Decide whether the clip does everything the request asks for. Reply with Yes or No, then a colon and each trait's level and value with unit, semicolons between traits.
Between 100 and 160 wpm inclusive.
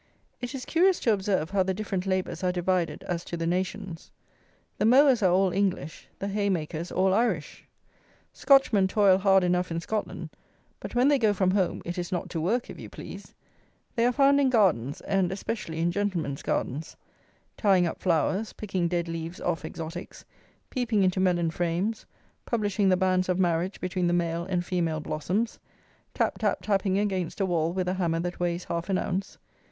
No: average, 185 wpm